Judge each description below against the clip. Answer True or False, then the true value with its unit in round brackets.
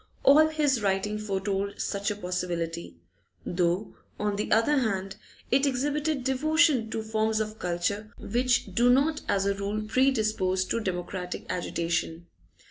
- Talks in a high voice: True (215 Hz)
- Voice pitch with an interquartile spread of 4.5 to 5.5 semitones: True (5.1 semitones)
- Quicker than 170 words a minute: False (135 wpm)